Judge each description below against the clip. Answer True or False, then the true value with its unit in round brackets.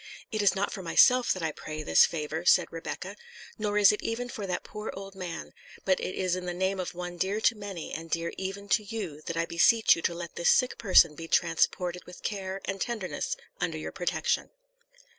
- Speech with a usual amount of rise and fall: True (3.2 semitones)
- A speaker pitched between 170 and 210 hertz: True (185 Hz)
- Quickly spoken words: True (215 wpm)